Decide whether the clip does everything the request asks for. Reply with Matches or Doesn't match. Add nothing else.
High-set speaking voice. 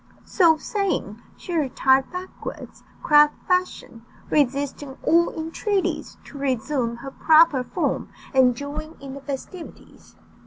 Matches